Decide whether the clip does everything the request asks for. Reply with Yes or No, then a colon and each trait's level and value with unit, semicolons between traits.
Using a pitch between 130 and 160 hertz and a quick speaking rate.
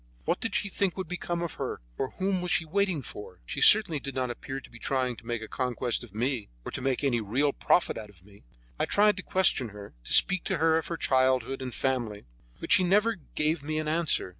Yes: low, 135 Hz; fast, 240 wpm